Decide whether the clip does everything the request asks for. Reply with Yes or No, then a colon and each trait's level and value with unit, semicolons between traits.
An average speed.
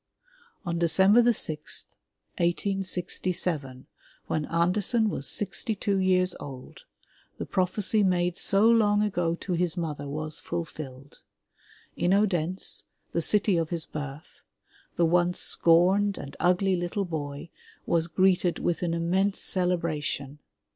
No: slow, 125 wpm